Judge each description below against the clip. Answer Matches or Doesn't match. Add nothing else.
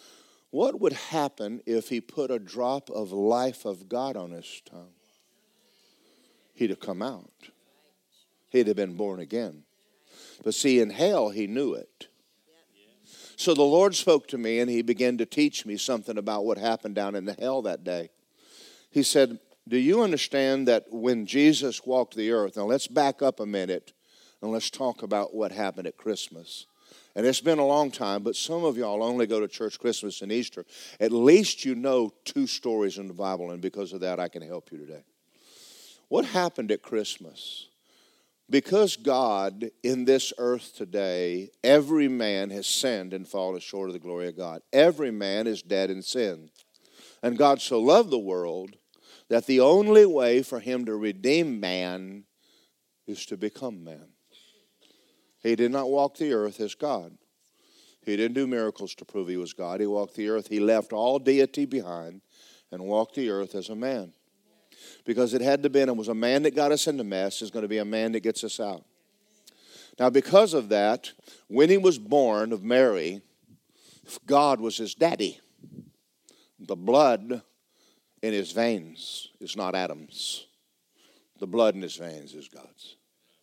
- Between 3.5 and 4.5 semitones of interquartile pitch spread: Doesn't match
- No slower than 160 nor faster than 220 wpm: Matches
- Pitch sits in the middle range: Doesn't match